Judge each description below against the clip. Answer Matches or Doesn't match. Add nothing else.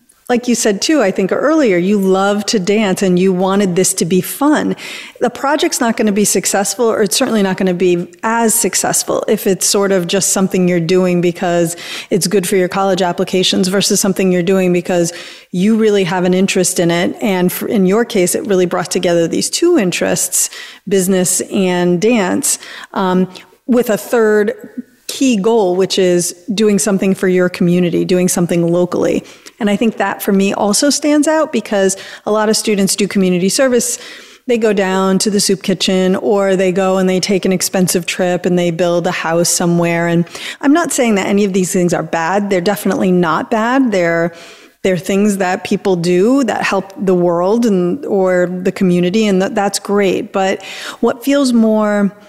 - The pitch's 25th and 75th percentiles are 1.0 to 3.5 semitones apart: Matches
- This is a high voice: Matches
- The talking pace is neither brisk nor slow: Matches